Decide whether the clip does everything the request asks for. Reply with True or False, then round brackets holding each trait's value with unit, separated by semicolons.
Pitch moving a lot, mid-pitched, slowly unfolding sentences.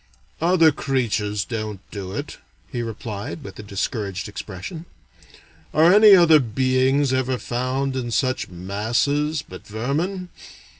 False (5.8 semitones; 130 Hz; 120 wpm)